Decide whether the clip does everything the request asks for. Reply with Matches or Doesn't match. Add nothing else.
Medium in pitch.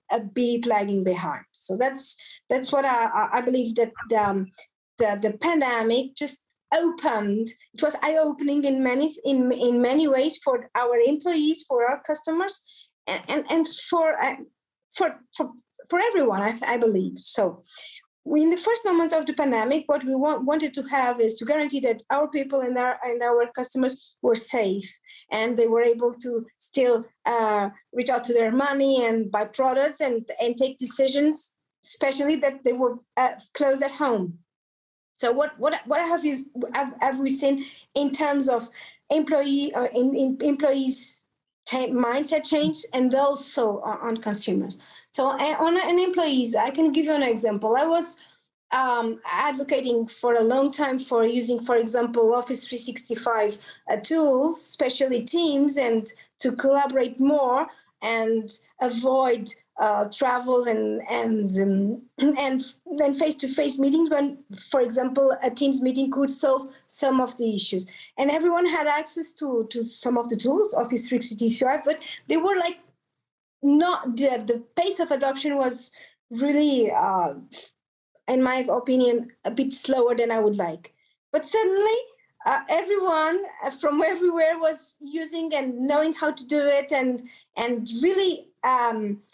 Doesn't match